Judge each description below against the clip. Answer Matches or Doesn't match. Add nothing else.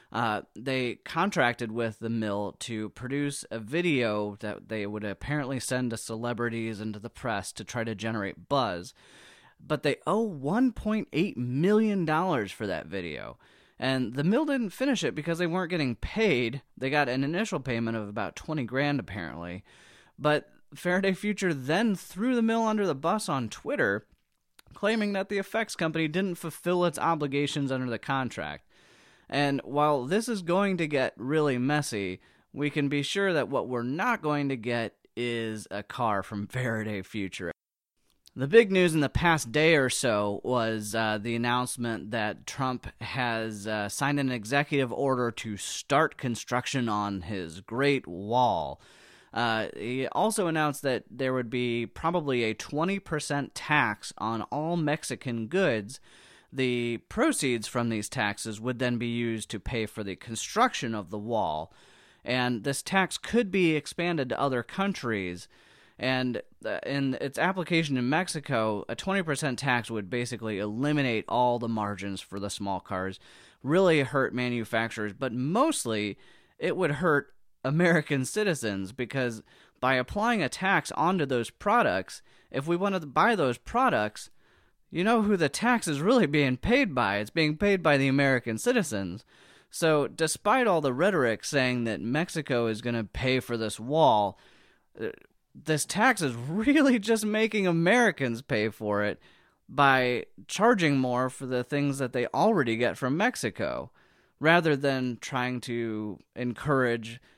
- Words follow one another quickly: Doesn't match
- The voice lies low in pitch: Matches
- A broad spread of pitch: Matches